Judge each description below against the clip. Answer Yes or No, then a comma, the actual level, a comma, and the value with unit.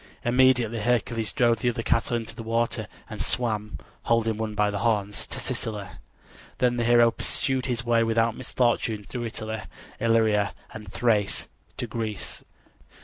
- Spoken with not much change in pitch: Yes, narrow, 1.8 semitones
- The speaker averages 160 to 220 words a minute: No, average, 150 wpm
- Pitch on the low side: Yes, low, 115 Hz